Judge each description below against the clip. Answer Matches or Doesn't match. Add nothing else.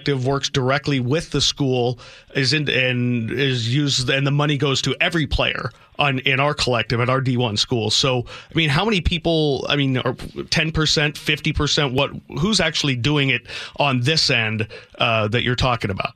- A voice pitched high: Doesn't match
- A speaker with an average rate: Matches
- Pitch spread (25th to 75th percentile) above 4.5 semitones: Doesn't match